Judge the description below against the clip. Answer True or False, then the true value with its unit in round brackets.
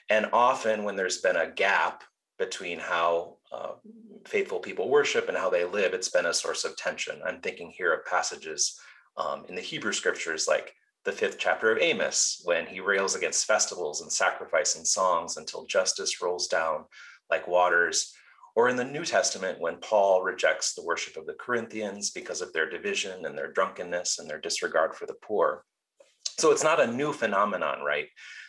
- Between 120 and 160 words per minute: False (185 wpm)